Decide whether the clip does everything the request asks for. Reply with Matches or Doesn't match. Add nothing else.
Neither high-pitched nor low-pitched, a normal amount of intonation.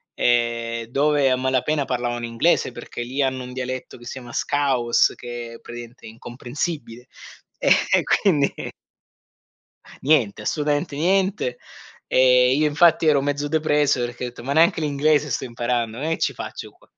Doesn't match